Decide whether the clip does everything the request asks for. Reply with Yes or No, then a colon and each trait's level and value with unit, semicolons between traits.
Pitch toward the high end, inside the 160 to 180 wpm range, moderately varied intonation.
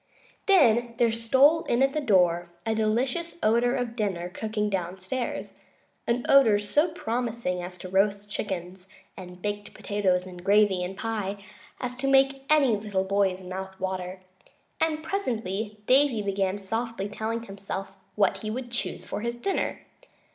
No: high, 210 Hz; average, 150 wpm; average, 4.2 semitones